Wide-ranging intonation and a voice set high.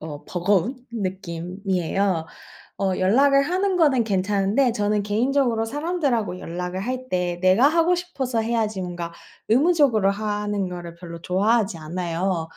Yes: wide, 5.9 semitones; high, 205 Hz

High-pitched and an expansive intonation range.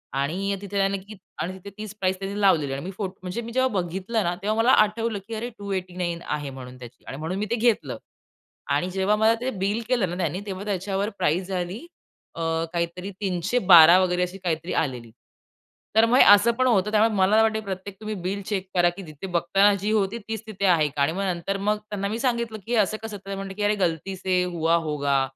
No: high, 195 Hz; average, 3.2 semitones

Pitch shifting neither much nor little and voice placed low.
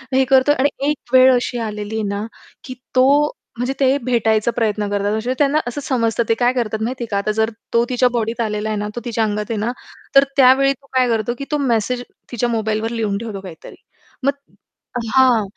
No: average, 3.1 semitones; high, 235 Hz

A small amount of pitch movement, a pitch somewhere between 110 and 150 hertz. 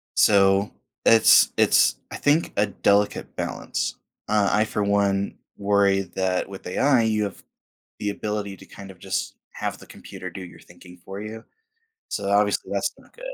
No: narrow, 1.4 semitones; low, 100 Hz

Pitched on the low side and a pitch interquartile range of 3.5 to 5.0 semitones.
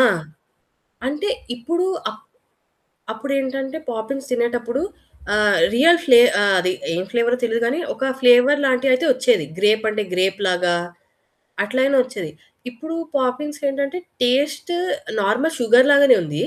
No: very high, 250 Hz; average, 4.0 semitones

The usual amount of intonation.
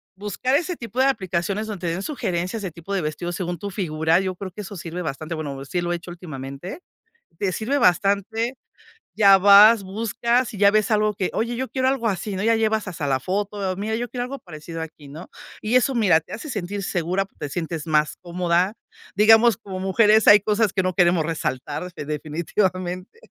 Yes: average, 4.1 semitones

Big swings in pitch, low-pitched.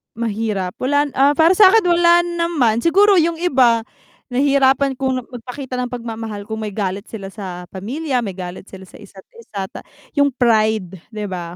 No: wide, 6.0 semitones; high, 235 Hz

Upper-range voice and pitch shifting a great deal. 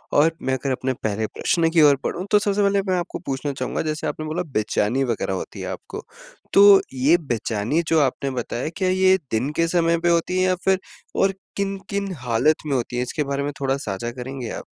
No: medium, 150 Hz; wide, 6.1 semitones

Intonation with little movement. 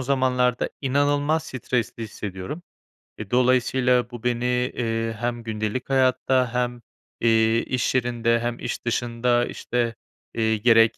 Yes: narrow, 1.8 semitones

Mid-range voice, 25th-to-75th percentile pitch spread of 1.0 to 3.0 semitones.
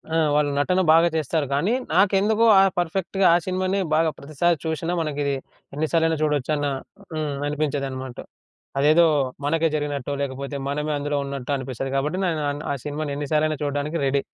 Yes: medium, 150 Hz; narrow, 2.6 semitones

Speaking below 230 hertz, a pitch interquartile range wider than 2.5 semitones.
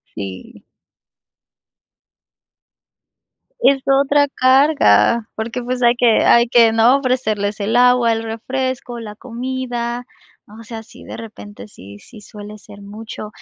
No: high, 235 Hz; average, 2.9 semitones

